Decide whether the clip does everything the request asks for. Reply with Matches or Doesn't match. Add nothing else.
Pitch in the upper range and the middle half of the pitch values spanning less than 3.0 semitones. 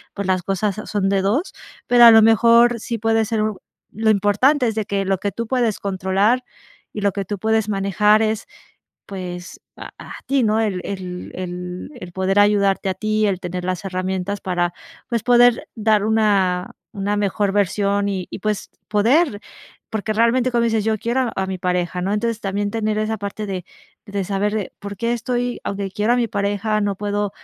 Matches